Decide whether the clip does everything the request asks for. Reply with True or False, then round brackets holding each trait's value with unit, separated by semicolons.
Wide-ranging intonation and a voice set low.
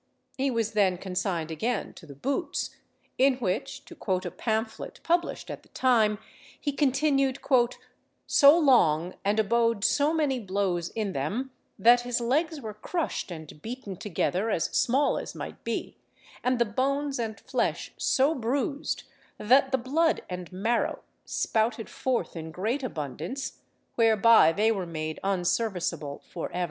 False (6.0 semitones; 225 Hz)